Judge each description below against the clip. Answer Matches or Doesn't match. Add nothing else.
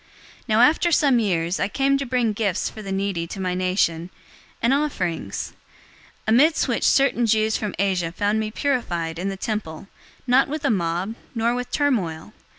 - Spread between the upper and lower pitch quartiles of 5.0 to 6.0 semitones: Matches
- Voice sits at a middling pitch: Doesn't match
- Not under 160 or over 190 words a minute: Matches